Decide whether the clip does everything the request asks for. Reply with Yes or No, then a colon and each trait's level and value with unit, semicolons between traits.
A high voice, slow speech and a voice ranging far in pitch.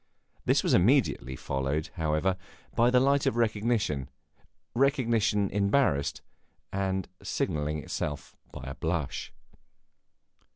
No: very low, 95 Hz; slow, 100 wpm; wide, 7.7 semitones